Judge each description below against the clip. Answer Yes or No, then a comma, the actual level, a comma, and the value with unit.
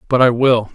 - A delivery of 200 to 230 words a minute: No, fast, 240 wpm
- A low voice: Yes, low, 120 Hz